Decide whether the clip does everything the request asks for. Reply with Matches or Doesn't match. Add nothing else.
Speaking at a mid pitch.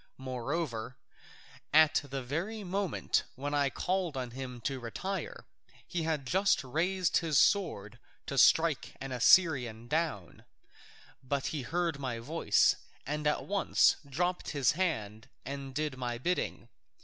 Matches